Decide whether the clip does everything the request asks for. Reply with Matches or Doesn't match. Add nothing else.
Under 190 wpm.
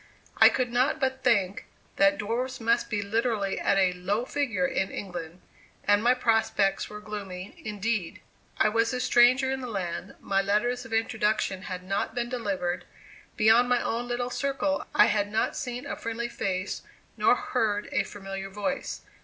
Matches